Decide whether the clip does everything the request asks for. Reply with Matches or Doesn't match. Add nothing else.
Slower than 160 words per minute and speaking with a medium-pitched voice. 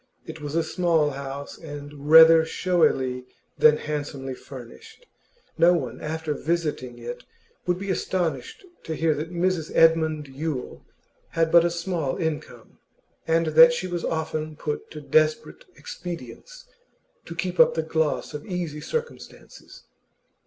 Matches